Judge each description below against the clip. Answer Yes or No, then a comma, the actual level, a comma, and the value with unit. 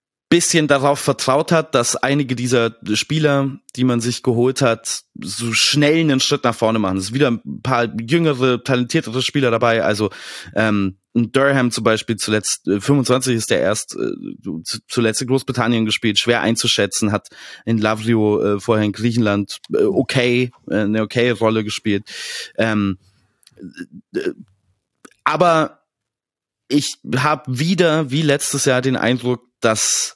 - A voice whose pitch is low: Yes, low, 120 Hz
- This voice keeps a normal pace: Yes, average, 140 wpm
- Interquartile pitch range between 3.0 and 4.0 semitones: Yes, average, 3.6 semitones